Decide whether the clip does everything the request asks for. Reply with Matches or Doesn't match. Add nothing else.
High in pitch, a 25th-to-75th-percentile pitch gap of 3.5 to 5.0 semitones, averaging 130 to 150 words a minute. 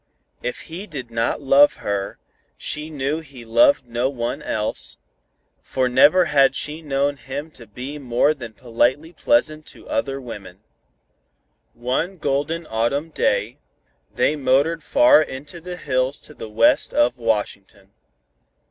Doesn't match